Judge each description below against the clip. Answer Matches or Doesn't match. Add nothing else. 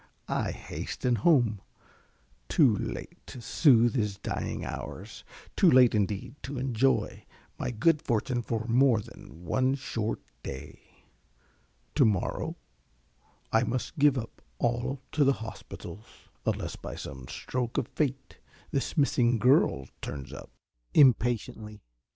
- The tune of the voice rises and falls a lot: Doesn't match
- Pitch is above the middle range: Doesn't match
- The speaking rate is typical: Doesn't match